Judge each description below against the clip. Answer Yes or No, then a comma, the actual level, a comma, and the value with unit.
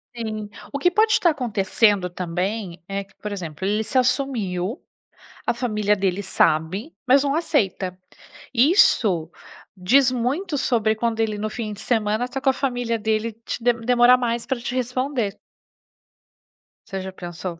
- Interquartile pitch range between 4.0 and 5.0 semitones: Yes, average, 4.3 semitones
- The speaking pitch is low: No, high, 225 Hz